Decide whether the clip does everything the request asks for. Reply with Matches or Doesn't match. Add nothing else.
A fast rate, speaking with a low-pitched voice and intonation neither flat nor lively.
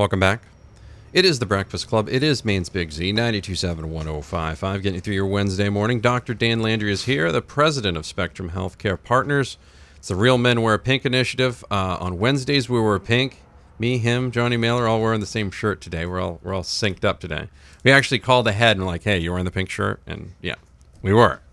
Matches